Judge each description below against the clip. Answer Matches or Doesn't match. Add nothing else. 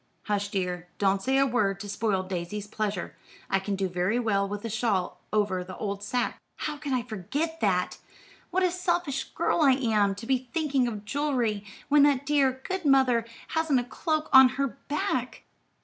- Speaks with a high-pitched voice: Matches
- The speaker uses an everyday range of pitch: Doesn't match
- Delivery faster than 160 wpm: Matches